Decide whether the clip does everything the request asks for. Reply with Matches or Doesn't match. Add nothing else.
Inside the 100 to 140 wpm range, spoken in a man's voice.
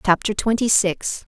Doesn't match